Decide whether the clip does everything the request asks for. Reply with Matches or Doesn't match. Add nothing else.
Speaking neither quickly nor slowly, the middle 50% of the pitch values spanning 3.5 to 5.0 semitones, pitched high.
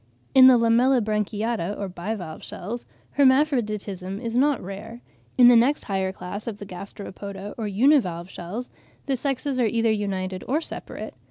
Matches